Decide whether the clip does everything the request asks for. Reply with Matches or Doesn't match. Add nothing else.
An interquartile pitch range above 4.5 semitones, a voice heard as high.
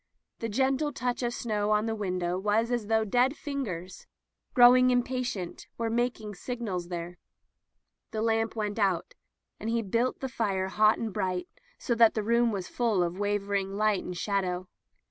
Doesn't match